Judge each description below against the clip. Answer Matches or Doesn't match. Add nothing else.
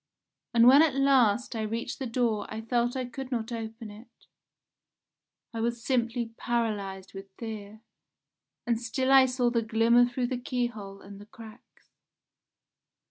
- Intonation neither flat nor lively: Doesn't match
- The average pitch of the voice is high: Matches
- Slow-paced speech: Doesn't match